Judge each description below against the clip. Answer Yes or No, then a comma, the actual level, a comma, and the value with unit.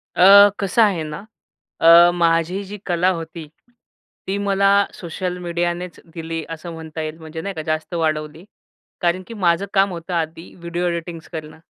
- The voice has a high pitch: No, medium, 170 Hz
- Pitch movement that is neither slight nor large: No, narrow, 2.2 semitones